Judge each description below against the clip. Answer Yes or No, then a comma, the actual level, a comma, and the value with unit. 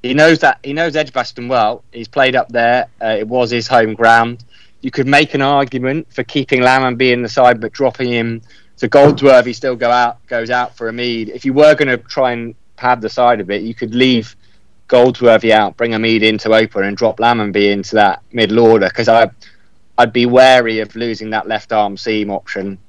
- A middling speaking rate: No, fast, 210 wpm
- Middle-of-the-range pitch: No, low, 120 Hz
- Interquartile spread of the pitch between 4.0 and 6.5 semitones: No, average, 2.7 semitones